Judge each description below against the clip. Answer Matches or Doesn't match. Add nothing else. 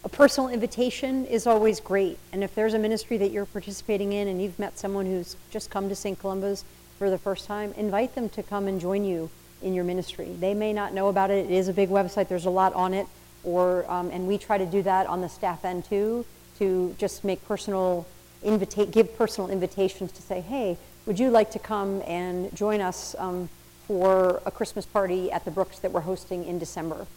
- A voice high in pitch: Matches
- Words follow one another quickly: Matches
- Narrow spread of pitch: Matches